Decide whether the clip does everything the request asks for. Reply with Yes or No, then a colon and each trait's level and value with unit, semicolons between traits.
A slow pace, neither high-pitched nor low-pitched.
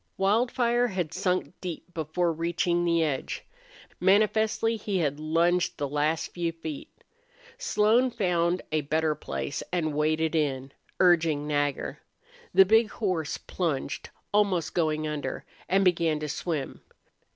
Yes: slow, 130 wpm; medium, 170 Hz